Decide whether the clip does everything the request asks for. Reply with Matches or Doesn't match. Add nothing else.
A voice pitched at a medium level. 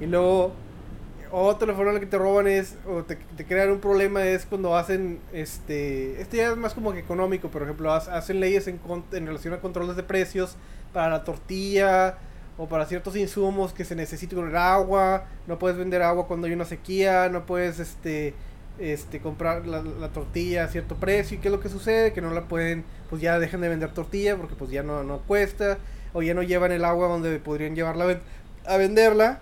Matches